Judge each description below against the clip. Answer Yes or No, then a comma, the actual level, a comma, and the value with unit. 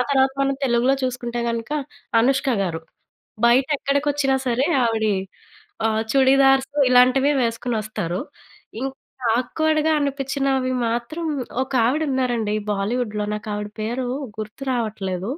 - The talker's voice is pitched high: Yes, very high, 250 Hz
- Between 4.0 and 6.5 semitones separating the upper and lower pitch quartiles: No, average, 3.5 semitones